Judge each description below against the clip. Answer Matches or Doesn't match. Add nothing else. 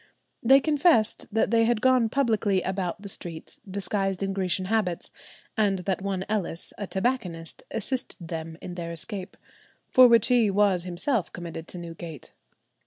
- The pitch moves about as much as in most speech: Matches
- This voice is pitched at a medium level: Doesn't match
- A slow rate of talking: Doesn't match